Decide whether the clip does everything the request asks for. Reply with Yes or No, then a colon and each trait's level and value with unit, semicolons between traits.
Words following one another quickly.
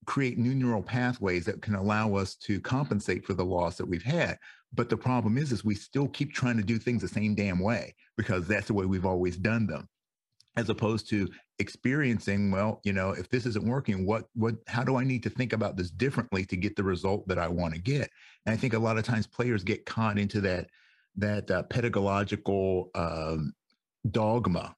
Yes: fast, 215 wpm